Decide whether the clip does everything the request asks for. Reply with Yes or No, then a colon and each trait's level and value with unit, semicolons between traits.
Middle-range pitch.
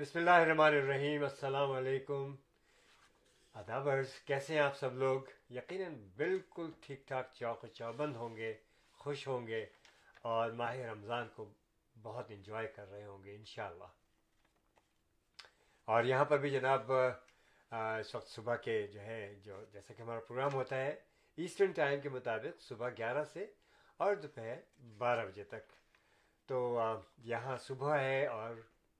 No: low, 130 Hz